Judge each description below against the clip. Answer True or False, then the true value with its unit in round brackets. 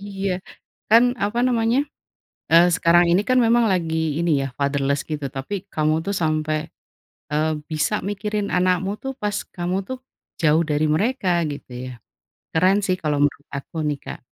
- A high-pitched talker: False (175 Hz)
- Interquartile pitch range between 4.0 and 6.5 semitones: True (5.0 semitones)